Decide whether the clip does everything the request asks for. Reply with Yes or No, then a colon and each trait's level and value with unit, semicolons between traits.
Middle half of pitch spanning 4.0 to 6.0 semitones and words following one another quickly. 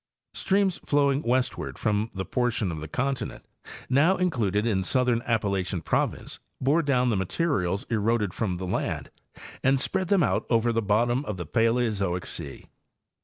No: average, 5.1 semitones; average, 160 wpm